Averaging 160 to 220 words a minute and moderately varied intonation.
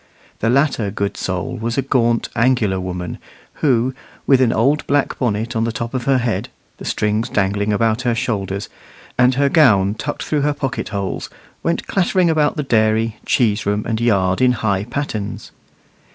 Yes: average, 175 wpm; average, 4.1 semitones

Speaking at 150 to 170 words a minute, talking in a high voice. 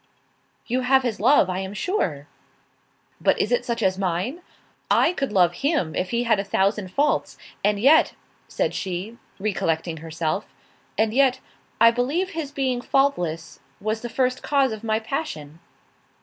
Yes: average, 160 wpm; high, 220 Hz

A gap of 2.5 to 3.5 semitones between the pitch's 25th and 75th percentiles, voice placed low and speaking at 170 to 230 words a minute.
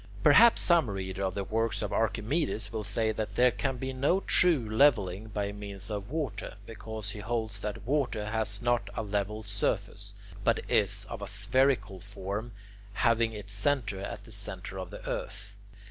Yes: average, 3.2 semitones; low, 110 Hz; average, 175 wpm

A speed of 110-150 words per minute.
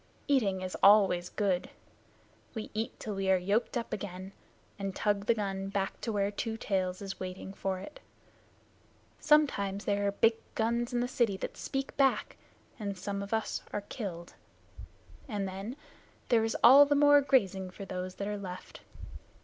No: average, 170 wpm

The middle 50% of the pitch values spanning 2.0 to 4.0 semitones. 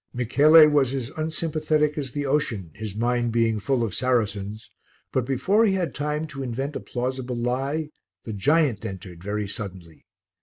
No: average, 5.3 semitones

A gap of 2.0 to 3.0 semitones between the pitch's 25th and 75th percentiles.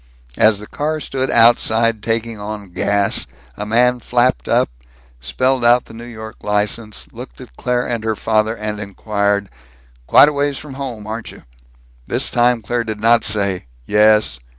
Yes: narrow, 2.6 semitones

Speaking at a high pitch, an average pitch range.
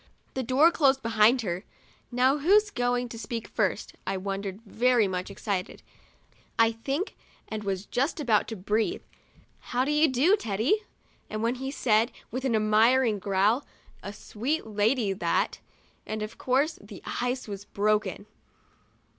Yes: high, 230 Hz; average, 4.1 semitones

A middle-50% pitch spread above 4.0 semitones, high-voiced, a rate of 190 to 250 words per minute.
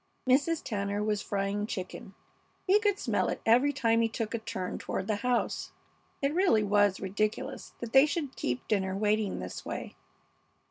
No: average, 4.6 semitones; high, 220 Hz; average, 170 wpm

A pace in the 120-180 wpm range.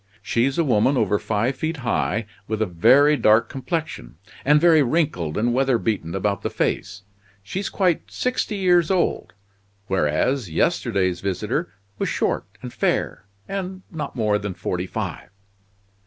Yes: average, 140 wpm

